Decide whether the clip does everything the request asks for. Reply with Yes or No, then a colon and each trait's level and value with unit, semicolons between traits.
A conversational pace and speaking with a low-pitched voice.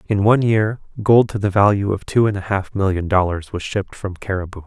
No: fast, 230 wpm; low, 100 Hz